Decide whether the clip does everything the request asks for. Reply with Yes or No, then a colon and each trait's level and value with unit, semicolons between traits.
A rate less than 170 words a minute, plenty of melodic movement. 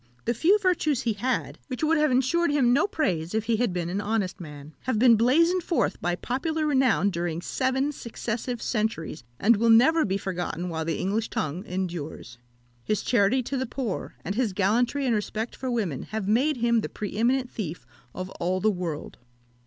No: average, 190 wpm; wide, 5.9 semitones